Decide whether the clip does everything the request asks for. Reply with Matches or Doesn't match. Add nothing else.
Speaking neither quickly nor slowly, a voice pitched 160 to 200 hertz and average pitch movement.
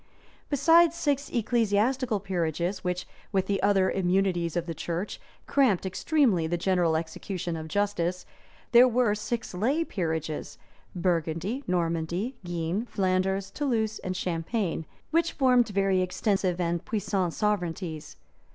Doesn't match